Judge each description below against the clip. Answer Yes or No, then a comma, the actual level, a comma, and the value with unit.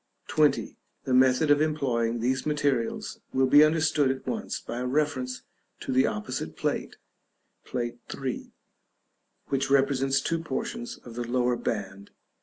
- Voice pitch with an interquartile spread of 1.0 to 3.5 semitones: Yes, average, 3.1 semitones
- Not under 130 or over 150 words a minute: Yes, average, 145 wpm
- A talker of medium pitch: No, low, 130 Hz